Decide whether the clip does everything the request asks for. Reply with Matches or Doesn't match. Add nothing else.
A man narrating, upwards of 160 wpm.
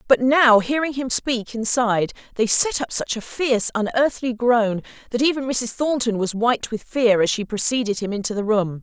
Doesn't match